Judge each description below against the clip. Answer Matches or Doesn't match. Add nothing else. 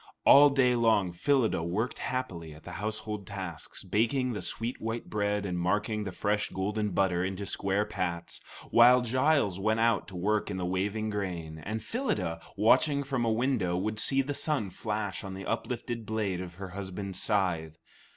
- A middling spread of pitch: Matches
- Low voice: Matches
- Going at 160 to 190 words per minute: Matches